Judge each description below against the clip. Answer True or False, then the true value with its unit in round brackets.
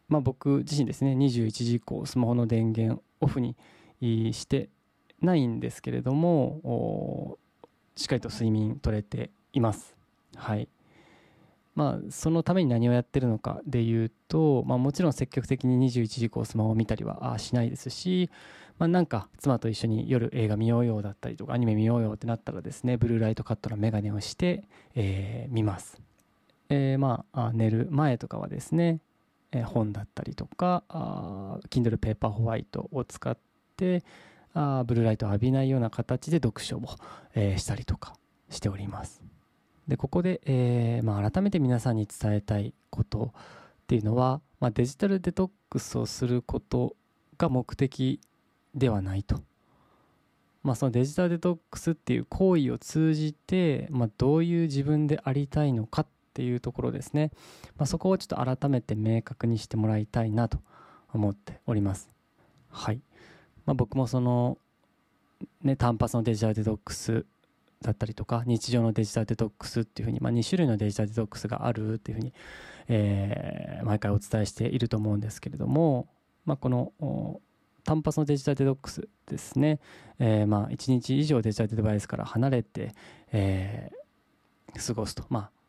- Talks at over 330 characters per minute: True (340 characters per minute)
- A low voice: True (120 Hz)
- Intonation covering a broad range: False (4.6 semitones)